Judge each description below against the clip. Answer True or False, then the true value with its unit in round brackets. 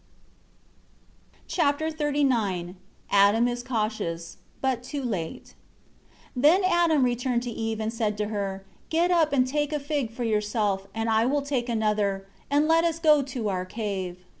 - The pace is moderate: True (160 wpm)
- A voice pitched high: True (240 Hz)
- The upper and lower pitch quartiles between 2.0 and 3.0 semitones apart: False (5.6 semitones)